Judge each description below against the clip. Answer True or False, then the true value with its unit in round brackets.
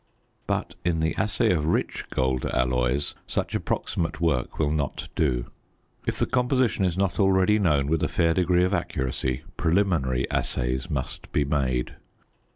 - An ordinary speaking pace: True (155 wpm)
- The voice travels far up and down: True (5.8 semitones)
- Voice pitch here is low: True (80 Hz)